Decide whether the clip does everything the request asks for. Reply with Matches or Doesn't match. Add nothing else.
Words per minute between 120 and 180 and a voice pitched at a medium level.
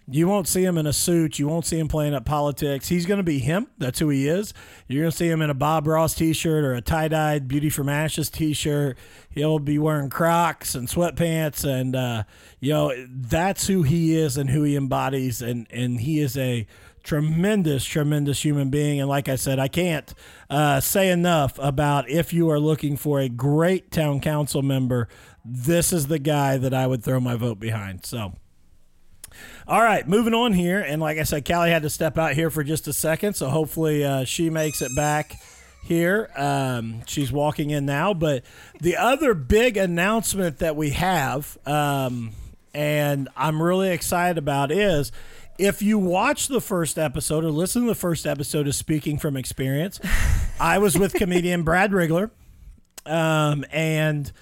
Doesn't match